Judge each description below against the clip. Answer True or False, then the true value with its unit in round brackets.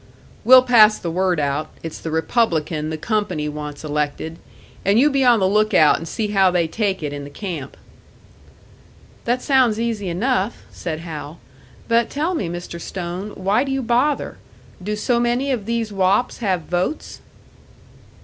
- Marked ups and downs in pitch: True (6.2 semitones)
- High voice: True (195 Hz)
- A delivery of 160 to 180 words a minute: True (165 wpm)